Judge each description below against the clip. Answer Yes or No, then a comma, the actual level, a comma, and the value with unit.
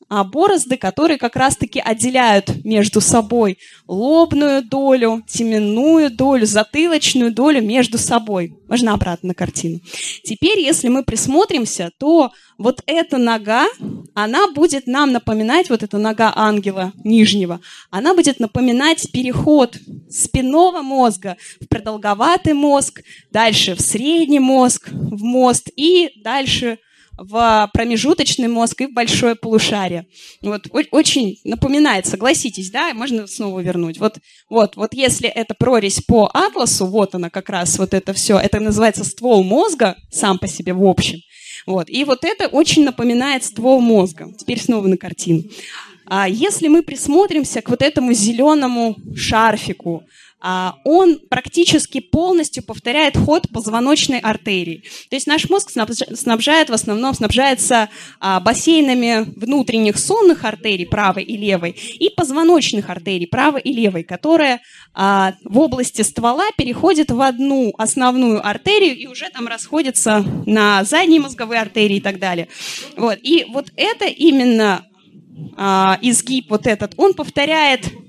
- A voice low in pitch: No, high, 235 Hz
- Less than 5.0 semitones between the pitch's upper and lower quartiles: No, average, 5.3 semitones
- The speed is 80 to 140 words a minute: Yes, average, 135 wpm